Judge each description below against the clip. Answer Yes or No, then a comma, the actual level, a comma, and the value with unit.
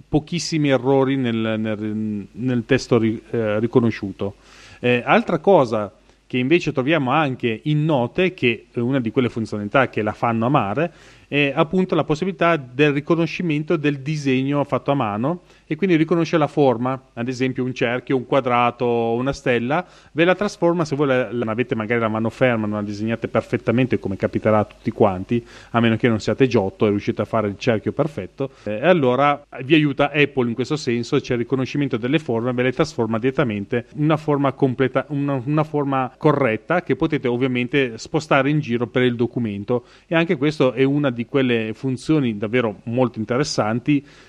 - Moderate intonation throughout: Yes, average, 4.0 semitones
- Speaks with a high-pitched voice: No, low, 130 Hz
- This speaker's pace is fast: Yes, fast, 175 wpm